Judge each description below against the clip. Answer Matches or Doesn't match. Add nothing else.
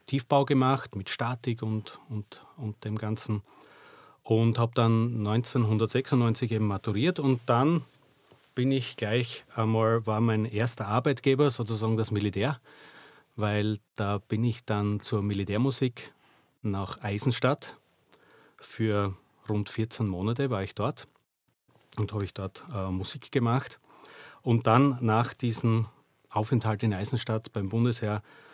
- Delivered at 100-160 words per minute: Matches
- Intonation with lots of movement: Doesn't match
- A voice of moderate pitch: Doesn't match